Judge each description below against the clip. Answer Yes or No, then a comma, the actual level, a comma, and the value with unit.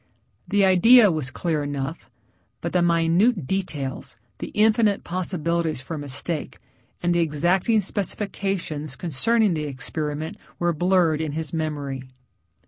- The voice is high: No, medium, 170 Hz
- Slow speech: Yes, slow, 125 wpm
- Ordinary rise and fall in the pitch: Yes, average, 4.1 semitones